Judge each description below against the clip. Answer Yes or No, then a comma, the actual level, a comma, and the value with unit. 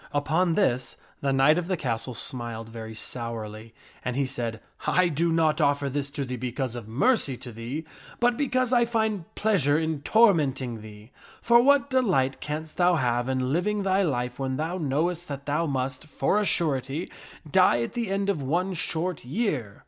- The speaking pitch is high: No, medium, 145 Hz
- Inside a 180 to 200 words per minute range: Yes, average, 185 wpm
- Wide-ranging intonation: Yes, wide, 6.3 semitones